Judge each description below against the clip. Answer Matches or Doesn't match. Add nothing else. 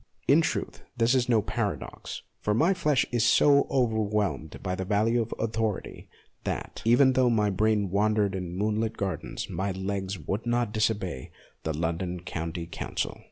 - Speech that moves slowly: Doesn't match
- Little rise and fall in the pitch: Doesn't match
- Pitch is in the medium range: Doesn't match